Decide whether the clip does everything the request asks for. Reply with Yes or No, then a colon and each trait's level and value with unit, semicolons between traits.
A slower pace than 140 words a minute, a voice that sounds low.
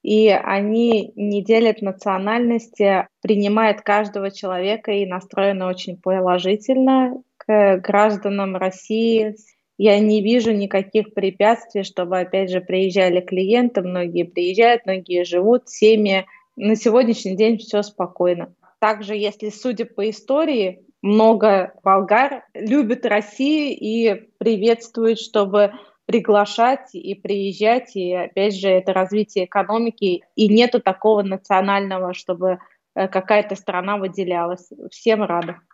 No: slow, 110 wpm; high, 205 Hz